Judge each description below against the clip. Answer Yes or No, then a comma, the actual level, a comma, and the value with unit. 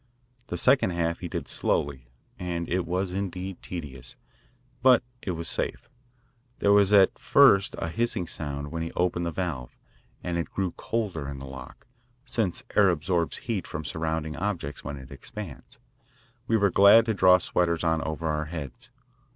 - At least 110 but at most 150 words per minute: No, average, 165 wpm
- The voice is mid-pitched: No, very low, 85 Hz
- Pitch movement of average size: Yes, average, 4.0 semitones